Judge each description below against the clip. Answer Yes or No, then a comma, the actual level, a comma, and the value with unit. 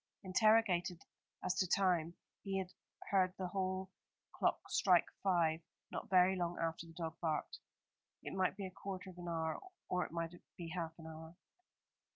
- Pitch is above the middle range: No, medium, 180 Hz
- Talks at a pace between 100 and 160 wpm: No, average, 170 wpm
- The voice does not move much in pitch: Yes, narrow, 2.2 semitones